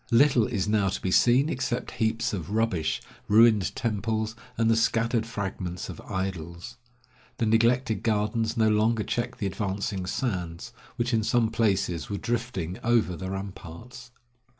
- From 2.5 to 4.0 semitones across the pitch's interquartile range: Yes, average, 3.3 semitones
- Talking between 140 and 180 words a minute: Yes, average, 150 wpm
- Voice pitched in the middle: No, low, 110 Hz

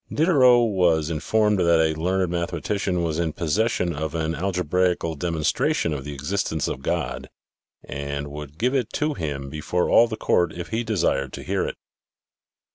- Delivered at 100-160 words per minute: No, average, 170 wpm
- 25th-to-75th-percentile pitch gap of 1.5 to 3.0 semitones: No, average, 4.3 semitones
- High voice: No, very low, 85 Hz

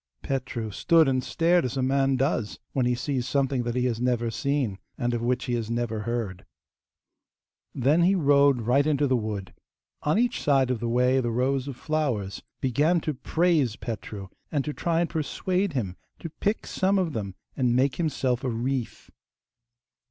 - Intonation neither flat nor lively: Yes, average, 3.8 semitones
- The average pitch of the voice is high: No, low, 130 Hz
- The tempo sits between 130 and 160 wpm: No, average, 180 wpm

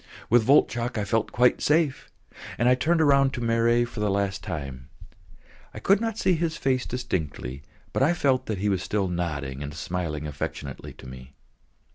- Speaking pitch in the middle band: No, low, 110 Hz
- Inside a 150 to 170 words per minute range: No, average, 180 wpm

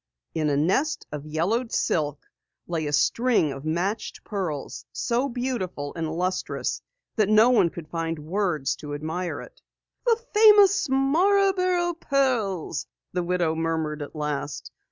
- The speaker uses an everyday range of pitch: No, wide, 8.7 semitones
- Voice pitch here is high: No, medium, 180 Hz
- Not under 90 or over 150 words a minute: Yes, slow, 135 wpm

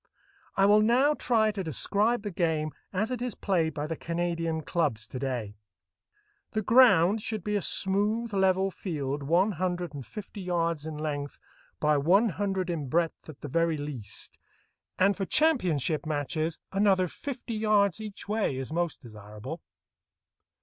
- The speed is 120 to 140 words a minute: No, average, 155 wpm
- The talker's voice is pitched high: No, medium, 175 Hz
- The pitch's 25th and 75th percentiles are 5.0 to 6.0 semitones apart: Yes, average, 5.3 semitones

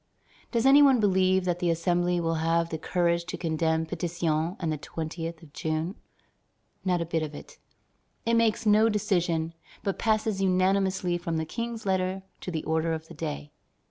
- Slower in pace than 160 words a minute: No, average, 175 wpm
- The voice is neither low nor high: Yes, medium, 175 Hz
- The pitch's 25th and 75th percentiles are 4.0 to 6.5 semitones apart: No, average, 3.0 semitones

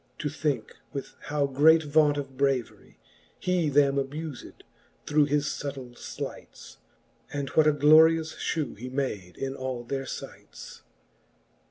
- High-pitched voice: No, medium, 145 Hz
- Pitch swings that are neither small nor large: No, narrow, 2.1 semitones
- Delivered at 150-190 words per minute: No, slow, 135 wpm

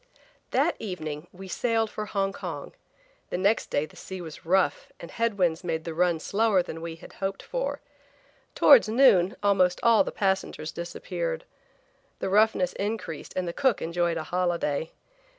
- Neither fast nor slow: Yes, average, 165 wpm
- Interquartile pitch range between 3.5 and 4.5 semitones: Yes, average, 3.9 semitones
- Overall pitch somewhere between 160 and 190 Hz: Yes, medium, 185 Hz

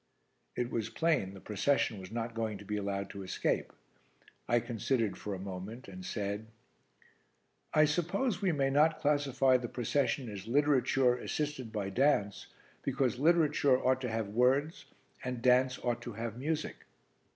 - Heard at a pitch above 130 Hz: No, low, 125 Hz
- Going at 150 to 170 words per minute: Yes, average, 155 wpm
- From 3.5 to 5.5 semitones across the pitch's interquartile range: Yes, average, 5.0 semitones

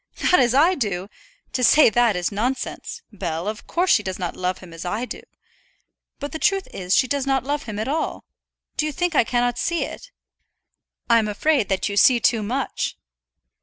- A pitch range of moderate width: No, wide, 6.1 semitones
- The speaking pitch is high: Yes, high, 240 Hz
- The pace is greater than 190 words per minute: Yes, average, 200 wpm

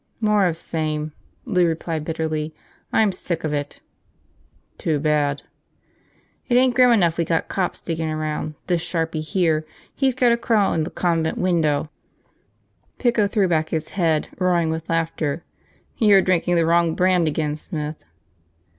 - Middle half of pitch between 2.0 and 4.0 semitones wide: Yes, average, 3.0 semitones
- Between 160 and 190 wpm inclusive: No, average, 145 wpm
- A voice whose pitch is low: No, medium, 165 Hz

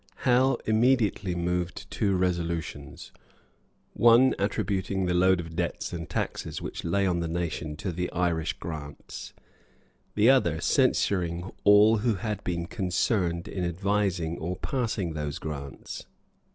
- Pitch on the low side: Yes, very low, 90 Hz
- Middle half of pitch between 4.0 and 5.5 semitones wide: No, average, 3.4 semitones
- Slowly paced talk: Yes, slow, 130 wpm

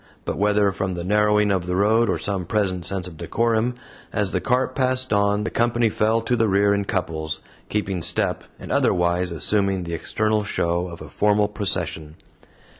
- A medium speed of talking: Yes, average, 185 wpm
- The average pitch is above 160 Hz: No, low, 100 Hz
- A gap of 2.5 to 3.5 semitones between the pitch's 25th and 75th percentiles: Yes, average, 3.0 semitones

